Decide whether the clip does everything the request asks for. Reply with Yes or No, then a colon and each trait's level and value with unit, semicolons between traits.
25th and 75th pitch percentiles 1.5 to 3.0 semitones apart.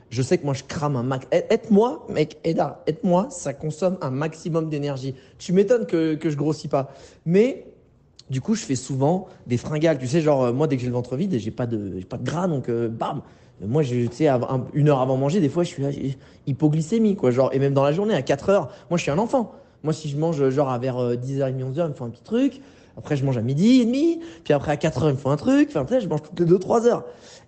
No: average, 5.1 semitones